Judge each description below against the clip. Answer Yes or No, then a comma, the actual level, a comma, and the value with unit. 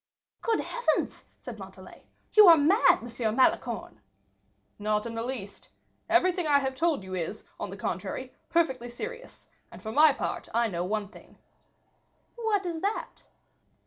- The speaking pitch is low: No, very high, 270 Hz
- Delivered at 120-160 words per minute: Yes, average, 155 wpm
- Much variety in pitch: Yes, wide, 8.3 semitones